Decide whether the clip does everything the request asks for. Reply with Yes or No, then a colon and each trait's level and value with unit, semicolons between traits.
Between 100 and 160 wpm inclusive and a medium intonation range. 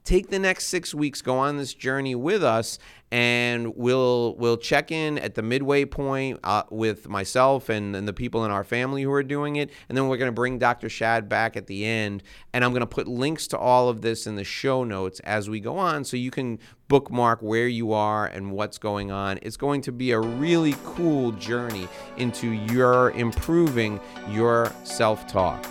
No: fast, 205 wpm; average, 3.4 semitones